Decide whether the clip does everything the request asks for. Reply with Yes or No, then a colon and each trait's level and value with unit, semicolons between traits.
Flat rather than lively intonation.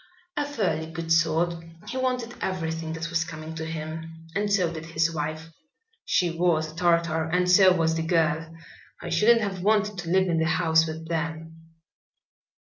Yes: narrow, 1.9 semitones